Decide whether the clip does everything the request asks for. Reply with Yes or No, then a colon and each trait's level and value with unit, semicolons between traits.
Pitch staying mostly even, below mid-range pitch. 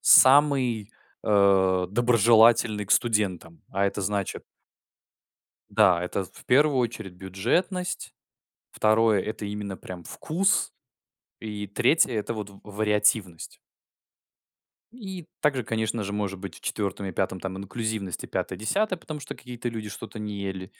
No: average, 3.4 semitones; low, 105 Hz